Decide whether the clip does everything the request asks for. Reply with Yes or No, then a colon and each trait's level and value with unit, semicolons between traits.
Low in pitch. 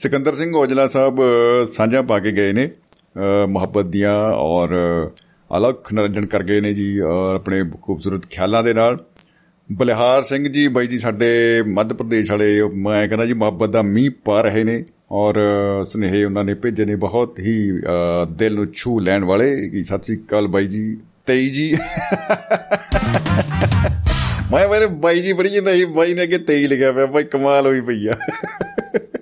Yes: low, 110 Hz